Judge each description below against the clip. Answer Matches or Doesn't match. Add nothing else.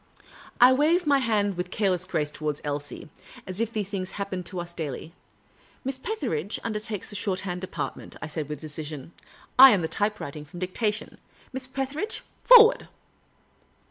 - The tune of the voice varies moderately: Doesn't match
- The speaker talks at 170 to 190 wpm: Matches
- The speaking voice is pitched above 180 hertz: Matches